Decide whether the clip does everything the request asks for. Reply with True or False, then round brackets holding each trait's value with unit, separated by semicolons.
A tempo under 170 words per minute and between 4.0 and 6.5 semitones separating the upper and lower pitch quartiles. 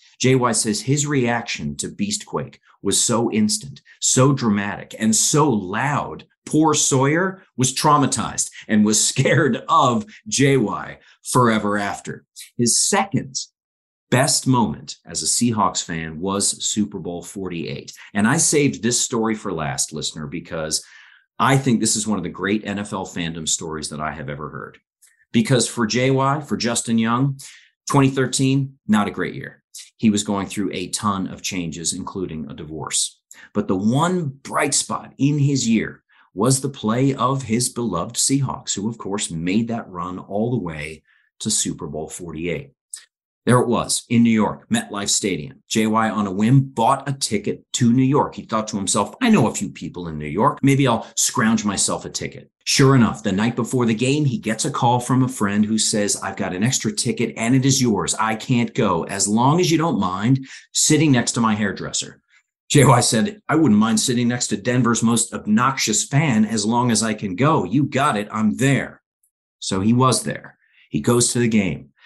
False (180 wpm; 4.5 semitones)